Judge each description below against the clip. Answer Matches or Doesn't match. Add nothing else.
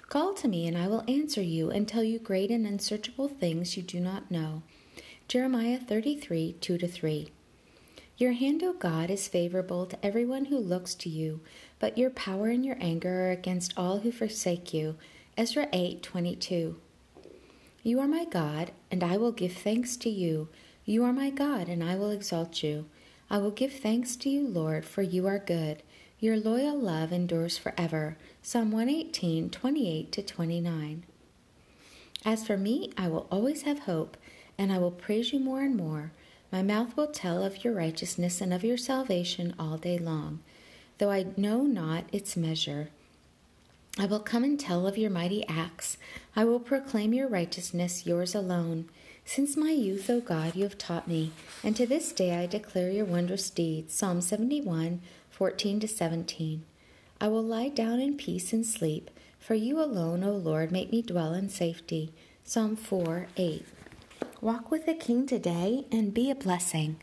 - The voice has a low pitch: Doesn't match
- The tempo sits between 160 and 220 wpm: Matches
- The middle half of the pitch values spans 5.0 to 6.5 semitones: Matches